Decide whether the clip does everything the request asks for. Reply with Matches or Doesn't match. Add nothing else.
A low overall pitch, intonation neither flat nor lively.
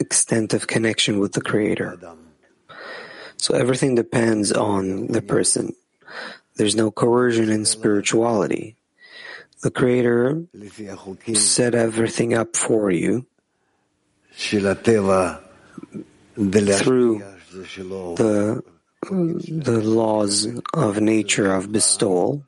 Matches